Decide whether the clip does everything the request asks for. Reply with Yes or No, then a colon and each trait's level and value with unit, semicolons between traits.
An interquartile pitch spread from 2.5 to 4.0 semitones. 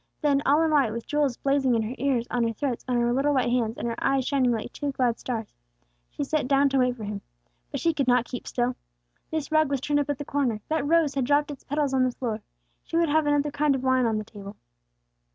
Yes: average, 3.2 semitones